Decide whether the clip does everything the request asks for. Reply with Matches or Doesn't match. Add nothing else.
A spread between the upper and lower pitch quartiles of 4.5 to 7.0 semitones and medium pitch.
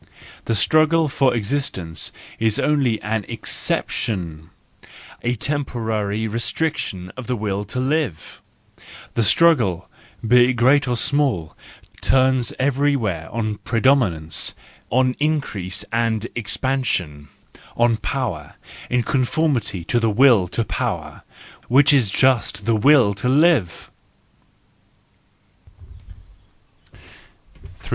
Doesn't match